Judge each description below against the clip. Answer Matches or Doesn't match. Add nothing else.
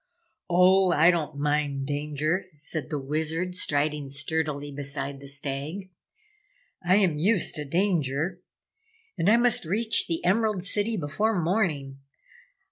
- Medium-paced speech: Doesn't match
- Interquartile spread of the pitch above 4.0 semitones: Matches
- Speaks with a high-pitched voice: Doesn't match